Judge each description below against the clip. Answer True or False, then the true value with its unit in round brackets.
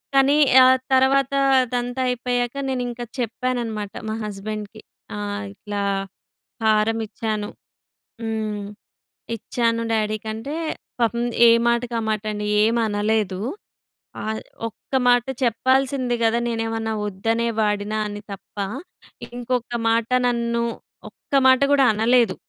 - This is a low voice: False (225 Hz)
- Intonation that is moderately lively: False (2.3 semitones)